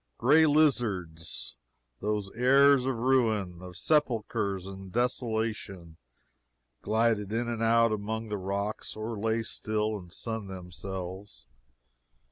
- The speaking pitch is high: No, low, 110 Hz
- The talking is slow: Yes, slow, 110 wpm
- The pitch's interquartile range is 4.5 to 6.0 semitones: No, average, 3.3 semitones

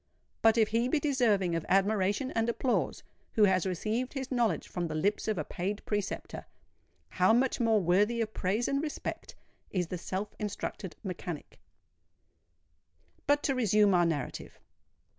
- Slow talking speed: No, average, 150 wpm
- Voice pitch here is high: Yes, high, 210 Hz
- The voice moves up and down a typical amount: Yes, average, 4.4 semitones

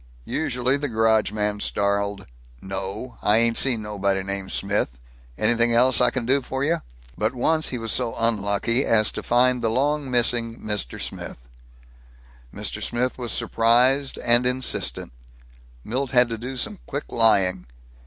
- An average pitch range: Yes, average, 3.4 semitones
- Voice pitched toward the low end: Yes, low, 115 Hz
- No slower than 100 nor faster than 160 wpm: Yes, average, 155 wpm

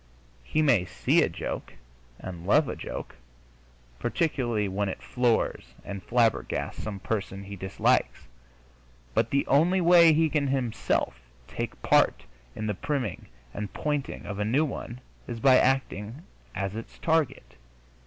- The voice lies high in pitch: No, low, 115 Hz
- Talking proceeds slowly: No, average, 145 wpm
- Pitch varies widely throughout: Yes, wide, 6.2 semitones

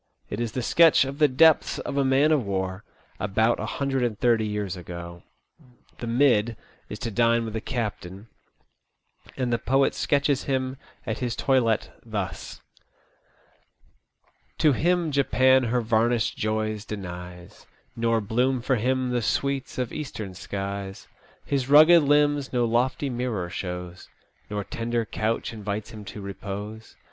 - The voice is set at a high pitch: No, low, 115 Hz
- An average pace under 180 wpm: Yes, average, 155 wpm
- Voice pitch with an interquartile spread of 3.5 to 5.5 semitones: Yes, average, 4.2 semitones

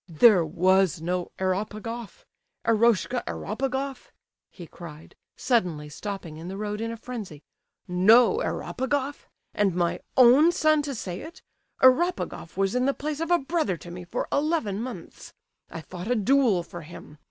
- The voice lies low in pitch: No, high, 215 Hz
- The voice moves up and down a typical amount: No, wide, 6.7 semitones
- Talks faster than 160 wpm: No, average, 155 wpm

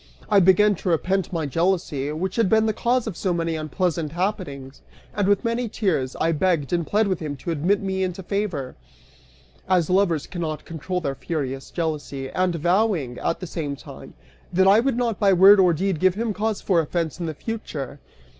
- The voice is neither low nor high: Yes, medium, 180 Hz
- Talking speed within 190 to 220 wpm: Yes, average, 195 wpm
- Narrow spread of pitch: No, average, 4.1 semitones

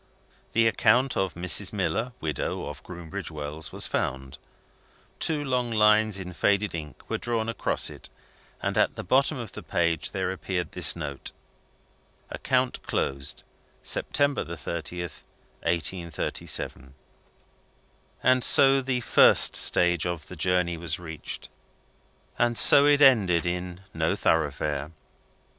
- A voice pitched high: No, very low, 90 Hz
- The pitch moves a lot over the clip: Yes, wide, 6.0 semitones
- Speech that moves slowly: Yes, slow, 125 wpm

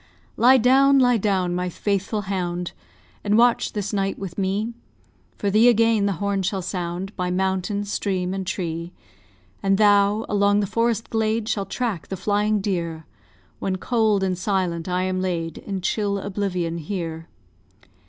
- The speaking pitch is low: No, high, 195 Hz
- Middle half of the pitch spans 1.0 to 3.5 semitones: Yes, narrow, 2.6 semitones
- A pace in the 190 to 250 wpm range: No, average, 155 wpm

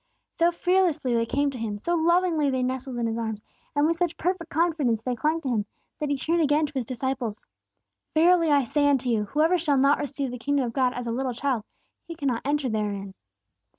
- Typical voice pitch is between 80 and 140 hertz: No, very high, 275 Hz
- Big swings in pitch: No, average, 4.7 semitones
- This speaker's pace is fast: Yes, fast, 220 wpm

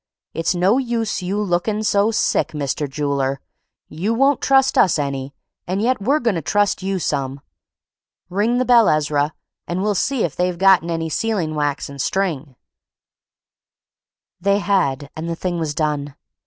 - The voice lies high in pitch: No, medium, 180 Hz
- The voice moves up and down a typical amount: No, wide, 5.9 semitones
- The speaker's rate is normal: Yes, average, 160 wpm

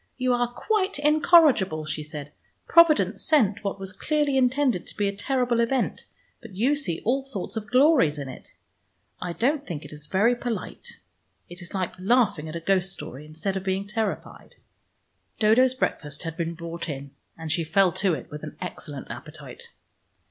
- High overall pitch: Yes, high, 200 Hz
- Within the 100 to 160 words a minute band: No, average, 175 wpm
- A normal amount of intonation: No, wide, 7.3 semitones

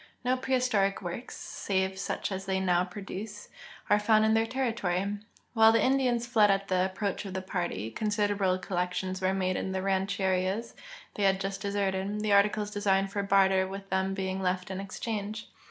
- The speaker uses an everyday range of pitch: No, narrow, 1.8 semitones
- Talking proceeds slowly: No, average, 180 wpm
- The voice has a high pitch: Yes, high, 195 Hz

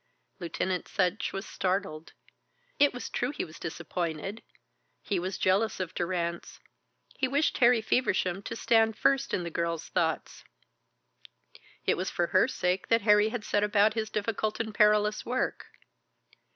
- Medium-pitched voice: No, high, 200 Hz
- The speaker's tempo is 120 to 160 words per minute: Yes, average, 150 wpm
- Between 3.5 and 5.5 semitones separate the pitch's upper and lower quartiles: Yes, average, 3.8 semitones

